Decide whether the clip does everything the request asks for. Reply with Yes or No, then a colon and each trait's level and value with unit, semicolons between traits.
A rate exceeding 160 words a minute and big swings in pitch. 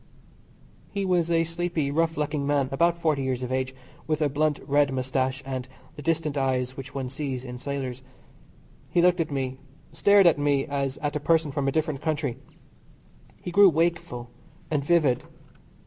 No: average, 175 wpm; average, 3.6 semitones